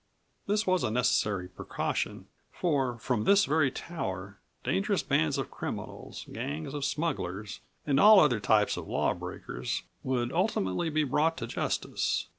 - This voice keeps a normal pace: Yes, average, 145 wpm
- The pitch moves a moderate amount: No, wide, 8.0 semitones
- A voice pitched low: Yes, low, 130 Hz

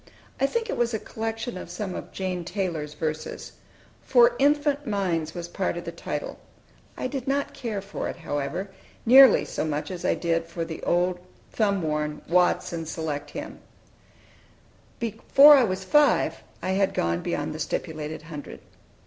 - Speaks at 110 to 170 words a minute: Yes, average, 165 wpm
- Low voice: No, medium, 185 Hz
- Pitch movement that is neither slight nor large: No, wide, 6.4 semitones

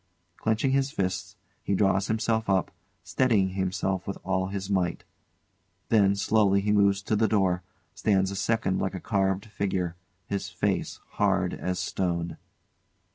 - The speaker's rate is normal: Yes, average, 145 wpm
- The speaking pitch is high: No, low, 100 Hz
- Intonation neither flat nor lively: No, narrow, 1.9 semitones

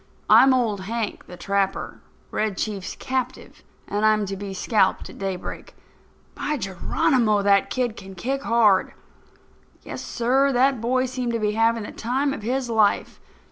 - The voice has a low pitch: No, high, 225 Hz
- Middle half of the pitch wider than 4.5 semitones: No, average, 4.1 semitones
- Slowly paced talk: No, average, 155 wpm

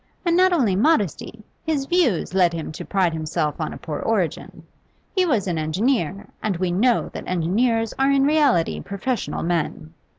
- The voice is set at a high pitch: Yes, high, 200 Hz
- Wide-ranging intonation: Yes, wide, 7.9 semitones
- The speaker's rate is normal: Yes, average, 170 wpm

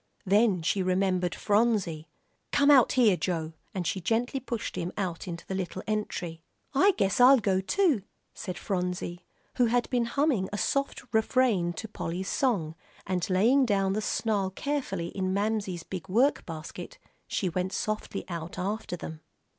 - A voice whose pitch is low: No, high, 195 Hz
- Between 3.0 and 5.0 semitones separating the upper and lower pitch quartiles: Yes, average, 4.5 semitones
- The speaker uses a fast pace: No, average, 160 wpm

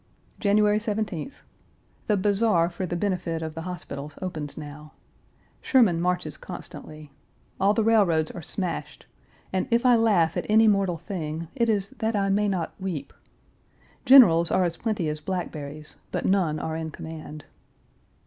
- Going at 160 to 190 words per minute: No, average, 150 wpm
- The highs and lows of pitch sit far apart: No, average, 4.6 semitones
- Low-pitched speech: No, medium, 180 Hz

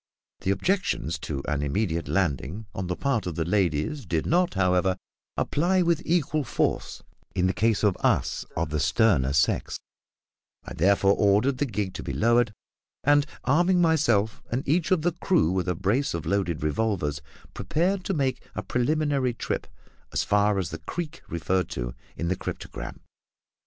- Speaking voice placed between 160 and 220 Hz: No, low, 105 Hz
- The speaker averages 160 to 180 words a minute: Yes, average, 165 wpm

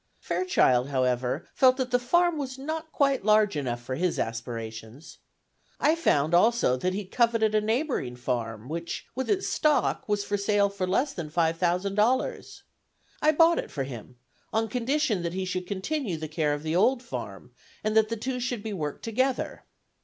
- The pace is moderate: Yes, average, 185 wpm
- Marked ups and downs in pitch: Yes, wide, 8.8 semitones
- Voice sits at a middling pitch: No, high, 205 Hz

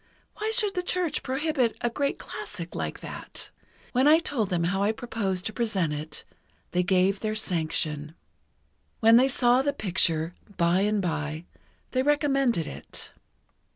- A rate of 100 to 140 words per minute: No, average, 155 wpm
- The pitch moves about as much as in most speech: No, wide, 7.3 semitones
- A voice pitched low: No, high, 215 Hz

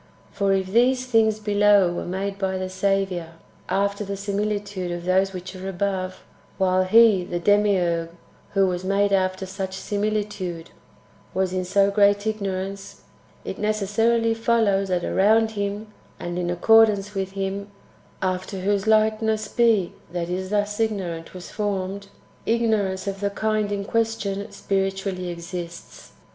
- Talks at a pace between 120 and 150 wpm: Yes, average, 145 wpm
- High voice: Yes, high, 195 Hz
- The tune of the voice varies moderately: No, narrow, 2.0 semitones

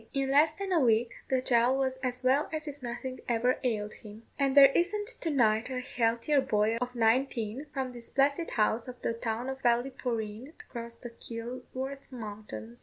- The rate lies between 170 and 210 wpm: Yes, average, 180 wpm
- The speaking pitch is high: Yes, very high, 250 Hz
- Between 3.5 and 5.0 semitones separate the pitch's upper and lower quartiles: No, average, 2.9 semitones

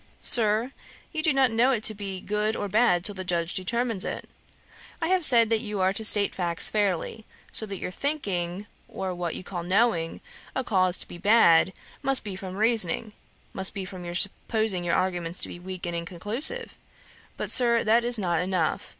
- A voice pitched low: No, high, 200 Hz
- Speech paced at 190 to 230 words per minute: Yes, average, 195 wpm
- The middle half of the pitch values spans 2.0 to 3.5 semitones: No, average, 4.2 semitones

